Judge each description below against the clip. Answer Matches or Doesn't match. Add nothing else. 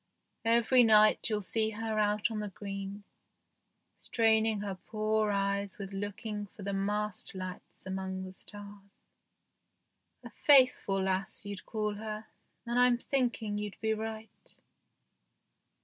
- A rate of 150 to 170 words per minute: Doesn't match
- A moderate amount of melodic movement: Doesn't match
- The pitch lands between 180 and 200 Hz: Doesn't match